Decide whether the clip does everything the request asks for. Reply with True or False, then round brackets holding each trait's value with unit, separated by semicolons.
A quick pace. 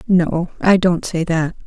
False (180 wpm)